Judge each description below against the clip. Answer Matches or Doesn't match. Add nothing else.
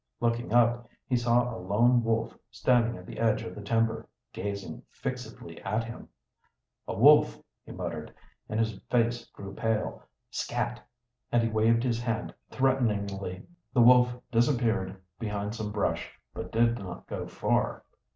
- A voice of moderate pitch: Doesn't match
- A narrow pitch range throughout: Matches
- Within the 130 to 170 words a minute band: Matches